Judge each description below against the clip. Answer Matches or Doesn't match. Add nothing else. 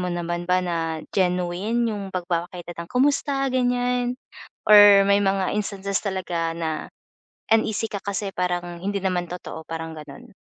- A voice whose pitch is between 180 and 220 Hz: Matches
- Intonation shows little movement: Doesn't match